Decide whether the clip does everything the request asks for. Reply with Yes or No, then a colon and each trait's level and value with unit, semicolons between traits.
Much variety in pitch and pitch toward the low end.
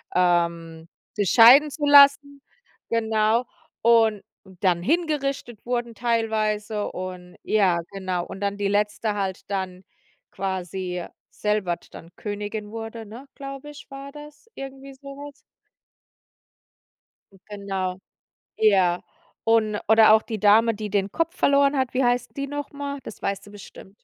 No: wide, 5.8 semitones; high, 215 Hz